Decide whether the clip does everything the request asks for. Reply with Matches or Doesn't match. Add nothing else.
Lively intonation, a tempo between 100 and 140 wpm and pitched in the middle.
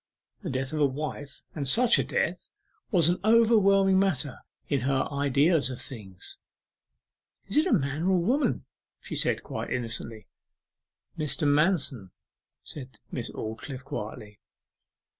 Matches